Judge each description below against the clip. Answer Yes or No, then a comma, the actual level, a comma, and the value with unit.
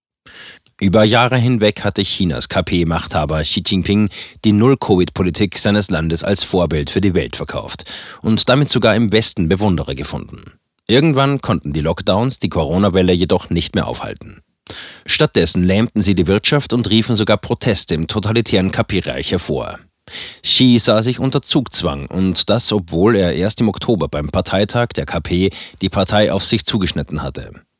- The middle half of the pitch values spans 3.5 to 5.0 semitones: Yes, average, 4.3 semitones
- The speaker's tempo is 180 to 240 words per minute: No, average, 150 wpm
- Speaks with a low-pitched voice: Yes, low, 100 Hz